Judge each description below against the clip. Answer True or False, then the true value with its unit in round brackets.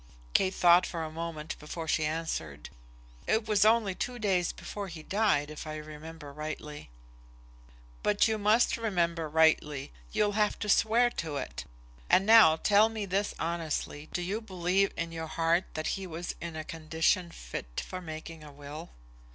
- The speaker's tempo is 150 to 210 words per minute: True (170 wpm)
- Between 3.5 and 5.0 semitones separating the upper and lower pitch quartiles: True (4.4 semitones)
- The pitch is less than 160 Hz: False (165 Hz)